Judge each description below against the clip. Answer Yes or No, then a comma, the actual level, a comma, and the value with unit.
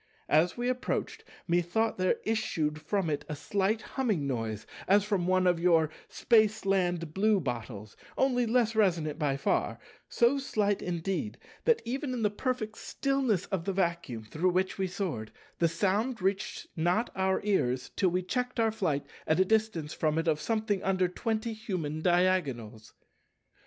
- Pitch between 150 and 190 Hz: Yes, medium, 185 Hz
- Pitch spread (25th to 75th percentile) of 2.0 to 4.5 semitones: No, average, 5.3 semitones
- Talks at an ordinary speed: Yes, average, 155 wpm